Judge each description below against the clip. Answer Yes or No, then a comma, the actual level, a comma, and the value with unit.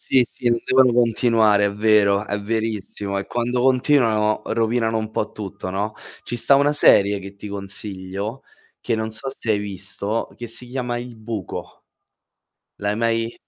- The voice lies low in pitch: Yes, low, 110 Hz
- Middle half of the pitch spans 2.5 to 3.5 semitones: Yes, average, 2.8 semitones